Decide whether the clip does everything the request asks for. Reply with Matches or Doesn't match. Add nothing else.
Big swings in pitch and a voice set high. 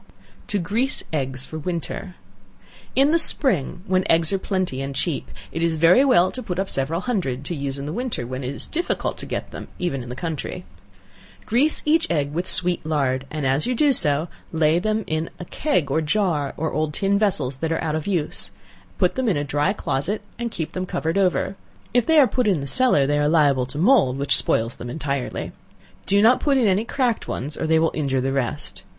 Doesn't match